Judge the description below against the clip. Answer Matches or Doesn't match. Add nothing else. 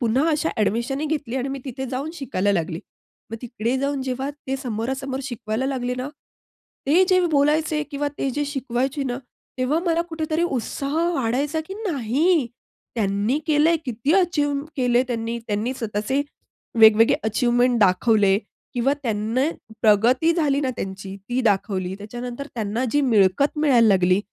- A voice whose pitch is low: Doesn't match